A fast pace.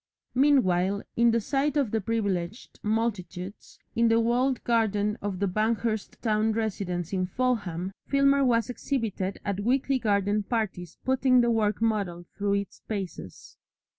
No: slow, 135 wpm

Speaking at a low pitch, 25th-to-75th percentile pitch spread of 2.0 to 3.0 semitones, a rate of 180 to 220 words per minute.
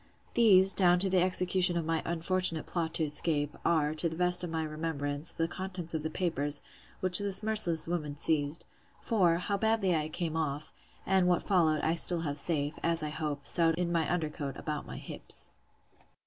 No: medium, 165 Hz; average, 2.7 semitones; average, 190 wpm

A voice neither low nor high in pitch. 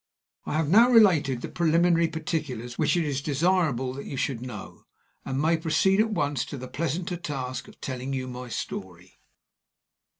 Yes: medium, 145 Hz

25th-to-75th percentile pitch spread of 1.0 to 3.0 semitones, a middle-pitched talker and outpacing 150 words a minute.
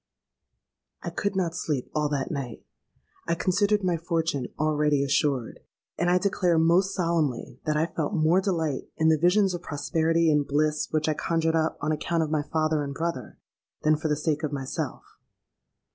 Yes: narrow, 2.4 semitones; medium, 160 Hz; average, 175 wpm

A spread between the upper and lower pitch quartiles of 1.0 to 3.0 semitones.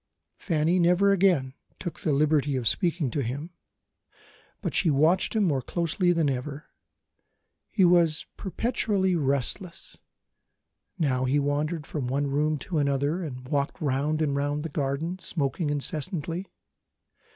No: average, 3.8 semitones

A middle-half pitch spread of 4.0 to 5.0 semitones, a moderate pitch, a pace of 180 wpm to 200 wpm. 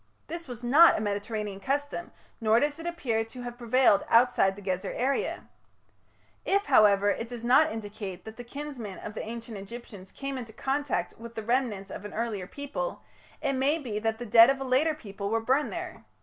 No: average, 4.4 semitones; high, 235 Hz; average, 195 wpm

